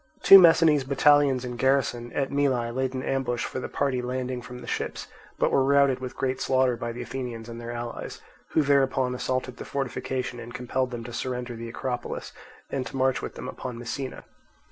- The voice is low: Yes, low, 130 Hz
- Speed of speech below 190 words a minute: No, average, 195 wpm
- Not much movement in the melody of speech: Yes, narrow, 1.6 semitones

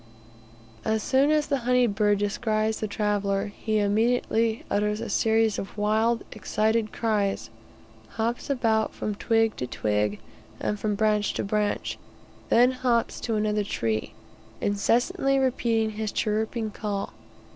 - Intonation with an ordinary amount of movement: No, narrow, 1.9 semitones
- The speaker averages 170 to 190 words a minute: No, slow, 135 wpm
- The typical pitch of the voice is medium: No, high, 215 Hz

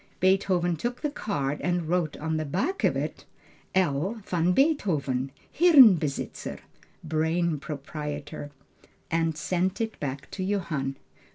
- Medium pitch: Yes, medium, 170 Hz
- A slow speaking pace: Yes, slow, 120 wpm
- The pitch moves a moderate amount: Yes, average, 4.3 semitones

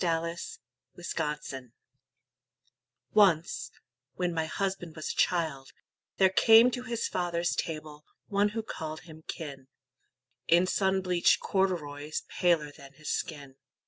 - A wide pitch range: No, average, 3.9 semitones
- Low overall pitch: No, medium, 170 Hz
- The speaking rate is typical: No, slow, 115 wpm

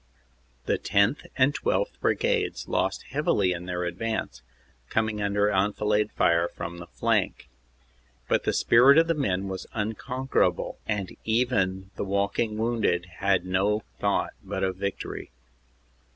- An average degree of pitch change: Yes, average, 3.7 semitones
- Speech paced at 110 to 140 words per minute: Yes, slow, 135 wpm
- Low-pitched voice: Yes, low, 105 Hz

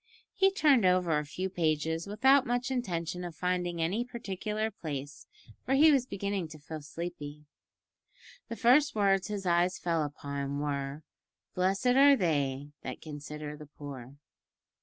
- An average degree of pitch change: No, wide, 6.4 semitones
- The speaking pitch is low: No, medium, 175 Hz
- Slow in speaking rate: No, average, 145 wpm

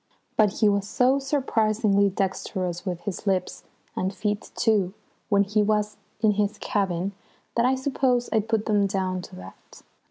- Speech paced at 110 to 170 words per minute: Yes, average, 160 wpm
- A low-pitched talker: No, high, 205 Hz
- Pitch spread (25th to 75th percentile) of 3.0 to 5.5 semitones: No, narrow, 2.4 semitones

